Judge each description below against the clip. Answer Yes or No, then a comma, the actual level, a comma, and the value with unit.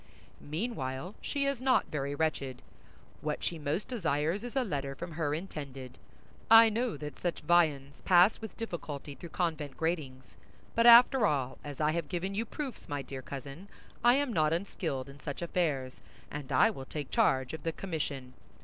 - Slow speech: No, average, 175 wpm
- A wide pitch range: Yes, wide, 6.0 semitones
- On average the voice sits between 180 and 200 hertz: No, medium, 160 Hz